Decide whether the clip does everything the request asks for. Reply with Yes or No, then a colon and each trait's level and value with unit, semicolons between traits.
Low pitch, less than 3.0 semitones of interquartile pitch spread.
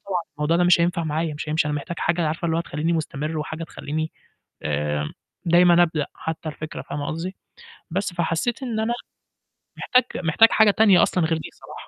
No: medium, 165 Hz; narrow, 2.4 semitones